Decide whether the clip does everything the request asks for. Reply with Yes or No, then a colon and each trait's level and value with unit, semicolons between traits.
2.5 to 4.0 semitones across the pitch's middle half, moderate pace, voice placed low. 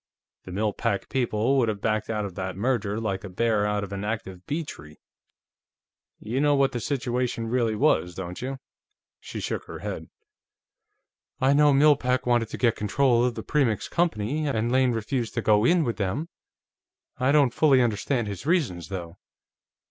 No: average, 4.6 semitones; average, 180 wpm; low, 115 Hz